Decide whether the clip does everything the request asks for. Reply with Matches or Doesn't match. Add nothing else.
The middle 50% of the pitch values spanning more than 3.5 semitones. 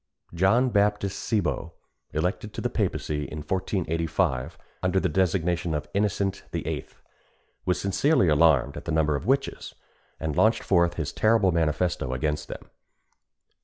Matches